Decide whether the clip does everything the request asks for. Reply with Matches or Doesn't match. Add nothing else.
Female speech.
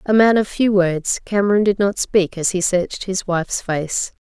Matches